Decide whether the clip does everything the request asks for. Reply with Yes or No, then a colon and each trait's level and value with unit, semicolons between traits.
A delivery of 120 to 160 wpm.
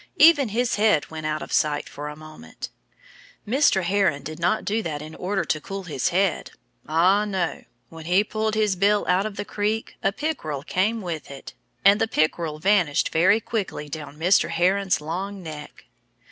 No: average, 180 wpm